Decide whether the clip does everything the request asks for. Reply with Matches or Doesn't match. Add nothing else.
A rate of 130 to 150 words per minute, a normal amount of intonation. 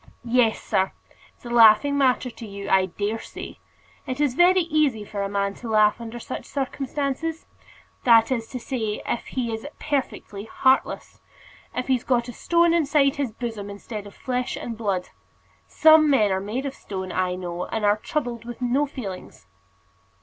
Doesn't match